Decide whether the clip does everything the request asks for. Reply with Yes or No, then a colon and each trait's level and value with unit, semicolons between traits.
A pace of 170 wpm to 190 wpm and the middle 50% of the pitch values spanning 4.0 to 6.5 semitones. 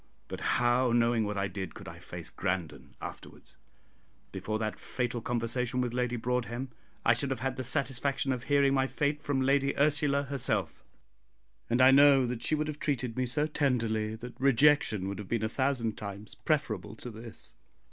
No: average, 180 wpm; average, 3.6 semitones